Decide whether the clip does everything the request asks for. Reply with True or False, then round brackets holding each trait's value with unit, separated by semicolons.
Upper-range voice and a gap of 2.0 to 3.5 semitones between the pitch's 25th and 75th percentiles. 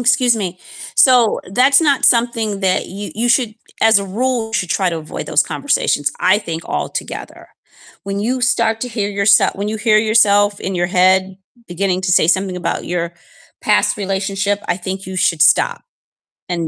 True (200 Hz; 3.2 semitones)